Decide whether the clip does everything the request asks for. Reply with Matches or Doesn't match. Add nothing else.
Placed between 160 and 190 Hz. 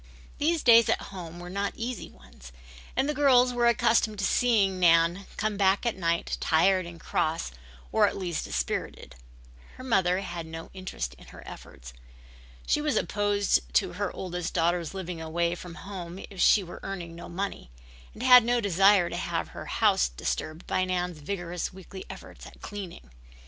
Matches